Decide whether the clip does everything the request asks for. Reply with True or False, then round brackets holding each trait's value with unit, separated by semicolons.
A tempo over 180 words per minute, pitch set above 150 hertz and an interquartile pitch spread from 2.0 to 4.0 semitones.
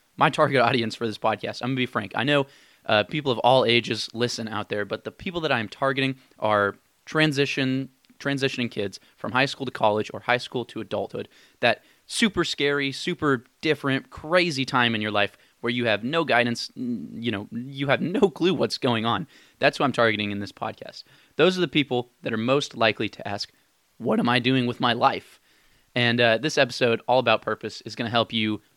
False (205 wpm; 125 Hz; 3.5 semitones)